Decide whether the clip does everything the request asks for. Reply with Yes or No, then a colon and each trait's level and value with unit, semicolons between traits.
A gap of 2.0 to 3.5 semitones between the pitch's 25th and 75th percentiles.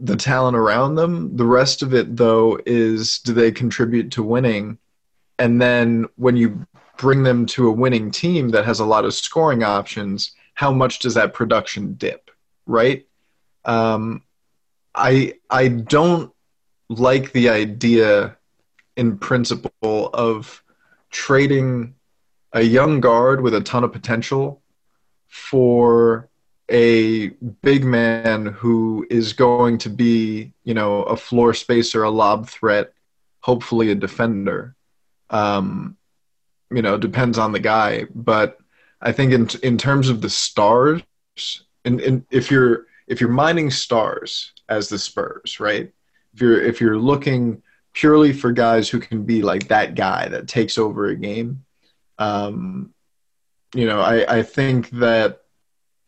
Yes: narrow, 2.4 semitones